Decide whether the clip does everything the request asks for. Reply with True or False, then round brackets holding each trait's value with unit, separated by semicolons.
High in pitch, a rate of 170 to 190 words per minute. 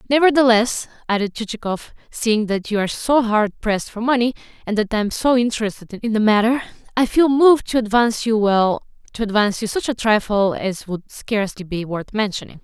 True (220 Hz; 185 wpm)